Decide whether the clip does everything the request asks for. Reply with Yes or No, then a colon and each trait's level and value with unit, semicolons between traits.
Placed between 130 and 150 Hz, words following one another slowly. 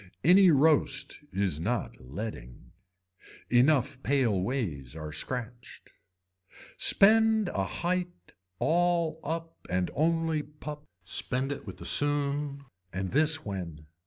Yes: medium, 140 Hz; slow, 110 wpm